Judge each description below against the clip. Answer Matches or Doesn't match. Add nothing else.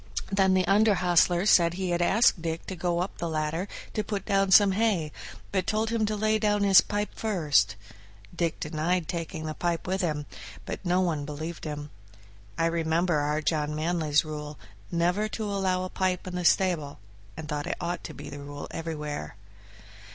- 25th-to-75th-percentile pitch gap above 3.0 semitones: Matches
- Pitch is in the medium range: Matches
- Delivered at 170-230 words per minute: Matches